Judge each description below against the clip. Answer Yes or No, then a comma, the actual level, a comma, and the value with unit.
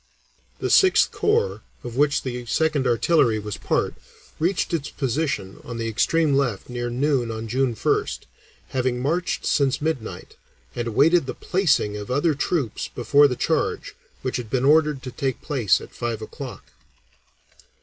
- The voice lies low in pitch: Yes, low, 130 Hz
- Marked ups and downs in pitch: No, average, 4.3 semitones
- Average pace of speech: Yes, average, 155 wpm